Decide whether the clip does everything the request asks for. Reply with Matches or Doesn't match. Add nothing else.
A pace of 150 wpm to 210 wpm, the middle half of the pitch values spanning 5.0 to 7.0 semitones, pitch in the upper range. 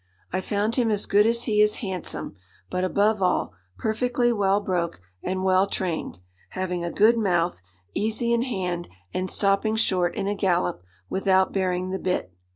Doesn't match